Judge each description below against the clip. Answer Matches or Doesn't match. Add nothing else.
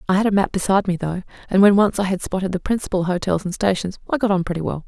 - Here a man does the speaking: Doesn't match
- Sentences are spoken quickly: Matches